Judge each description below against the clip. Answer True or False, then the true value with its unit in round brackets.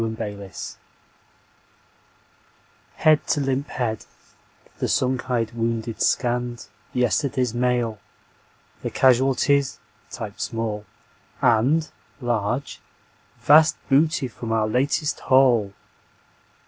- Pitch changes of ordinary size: True (3.0 semitones)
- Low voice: True (125 Hz)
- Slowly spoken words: True (95 wpm)